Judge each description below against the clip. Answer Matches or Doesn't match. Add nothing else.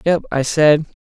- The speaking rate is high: Doesn't match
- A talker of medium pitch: Matches